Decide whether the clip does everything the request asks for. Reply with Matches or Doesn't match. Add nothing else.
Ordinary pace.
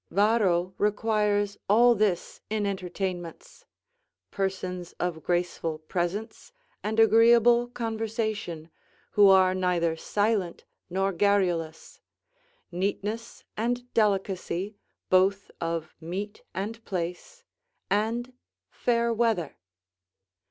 Doesn't match